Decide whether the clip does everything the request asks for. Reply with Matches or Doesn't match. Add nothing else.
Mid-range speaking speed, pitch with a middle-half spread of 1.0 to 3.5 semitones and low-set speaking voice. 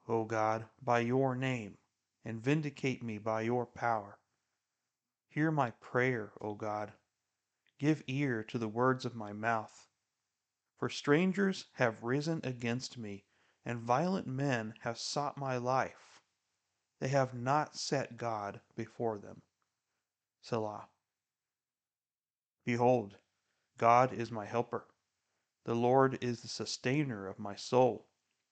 Doesn't match